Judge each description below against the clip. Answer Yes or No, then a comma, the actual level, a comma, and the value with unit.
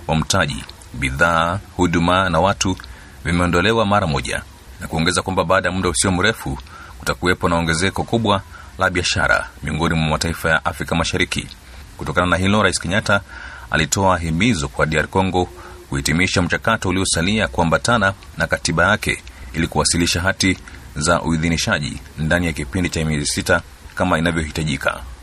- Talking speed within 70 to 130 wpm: No, fast, 140 wpm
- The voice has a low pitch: Yes, very low, 85 Hz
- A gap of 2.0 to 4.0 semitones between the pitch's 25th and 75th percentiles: Yes, average, 2.8 semitones